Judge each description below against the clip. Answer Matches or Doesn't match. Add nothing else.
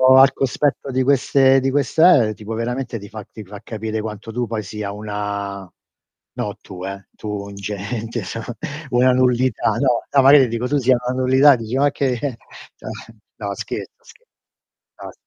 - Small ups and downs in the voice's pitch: Doesn't match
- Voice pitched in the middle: Doesn't match